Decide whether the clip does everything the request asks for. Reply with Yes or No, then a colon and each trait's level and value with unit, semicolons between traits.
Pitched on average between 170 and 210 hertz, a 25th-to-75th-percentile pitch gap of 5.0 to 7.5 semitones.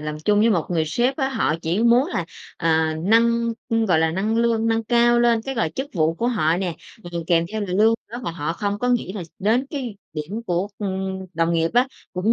Yes: high, 205 Hz; wide, 5.6 semitones